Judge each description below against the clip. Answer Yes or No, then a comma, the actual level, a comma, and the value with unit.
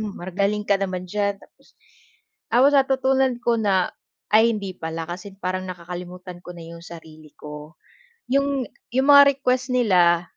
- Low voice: No, high, 190 Hz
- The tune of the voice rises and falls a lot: Yes, wide, 5.8 semitones